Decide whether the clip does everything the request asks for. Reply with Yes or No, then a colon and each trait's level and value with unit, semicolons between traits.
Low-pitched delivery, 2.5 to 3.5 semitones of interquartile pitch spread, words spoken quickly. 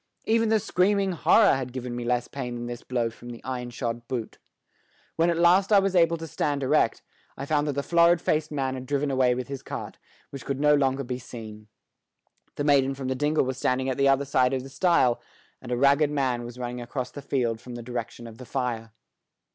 Yes: low, 130 Hz; average, 3.2 semitones; fast, 225 wpm